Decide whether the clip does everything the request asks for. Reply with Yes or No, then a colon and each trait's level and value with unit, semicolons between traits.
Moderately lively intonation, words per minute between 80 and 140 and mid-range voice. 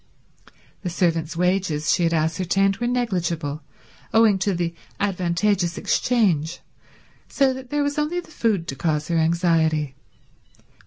Yes: average, 4.5 semitones; slow, 135 wpm; medium, 175 Hz